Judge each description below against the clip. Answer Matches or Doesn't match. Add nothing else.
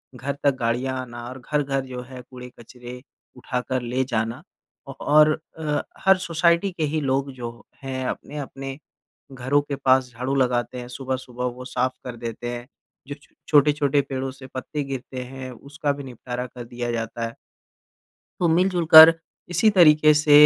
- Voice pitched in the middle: Doesn't match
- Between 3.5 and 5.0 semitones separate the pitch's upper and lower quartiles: Doesn't match